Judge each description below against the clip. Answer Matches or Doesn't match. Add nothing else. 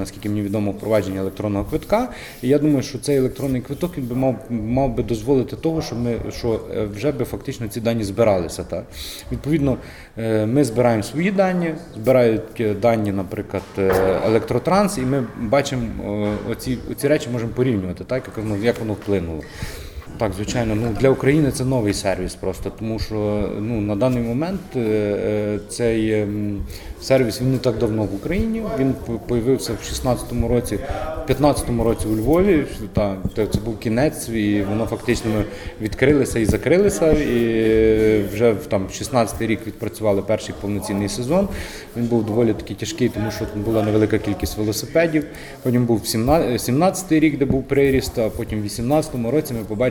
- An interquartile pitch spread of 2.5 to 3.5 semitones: Doesn't match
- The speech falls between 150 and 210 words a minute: Matches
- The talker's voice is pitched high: Doesn't match